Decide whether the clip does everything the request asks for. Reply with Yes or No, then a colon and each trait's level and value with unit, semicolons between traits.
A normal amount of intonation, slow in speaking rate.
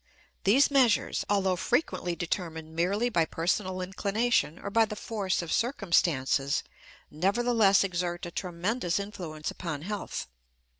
Yes: average, 3.7 semitones; slow, 120 wpm